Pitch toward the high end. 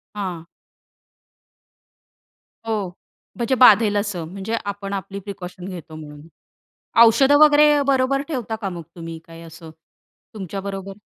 Yes: high, 200 Hz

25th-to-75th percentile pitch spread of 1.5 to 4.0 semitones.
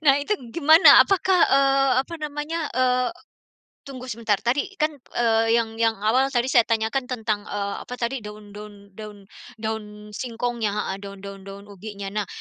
No: average, 4.4 semitones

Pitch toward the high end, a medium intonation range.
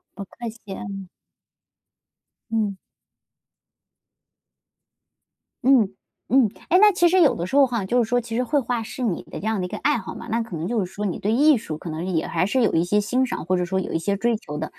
Yes: high, 220 Hz; average, 4.7 semitones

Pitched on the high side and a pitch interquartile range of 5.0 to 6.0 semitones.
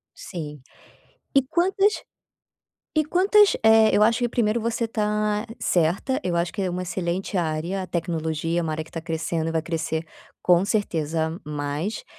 No: medium, 180 Hz; wide, 5.5 semitones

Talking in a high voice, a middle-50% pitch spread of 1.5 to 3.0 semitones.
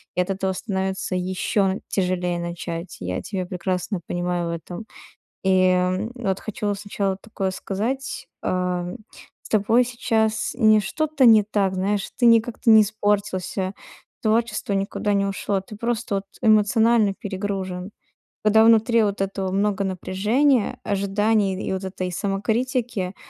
Yes: high, 200 Hz; average, 2.7 semitones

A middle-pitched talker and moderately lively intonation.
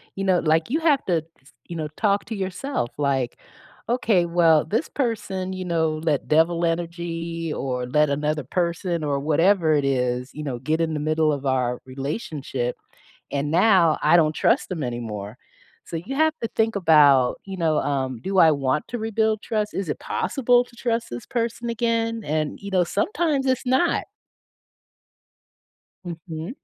No: medium, 165 Hz; wide, 6.3 semitones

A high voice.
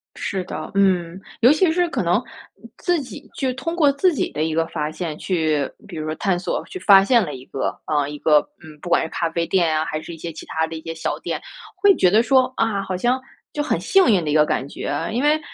No: medium, 180 Hz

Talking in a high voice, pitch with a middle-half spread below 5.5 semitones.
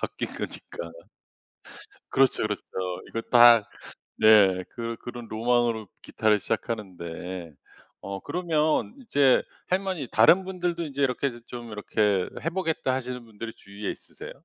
No: low, 120 Hz; average, 5.1 semitones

